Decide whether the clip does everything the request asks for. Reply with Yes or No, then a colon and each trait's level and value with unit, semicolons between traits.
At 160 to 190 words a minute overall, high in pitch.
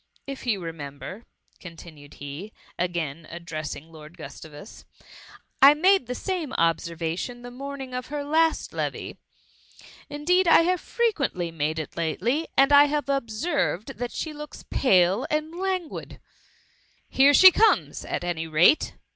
No: average, 145 wpm; high, 245 Hz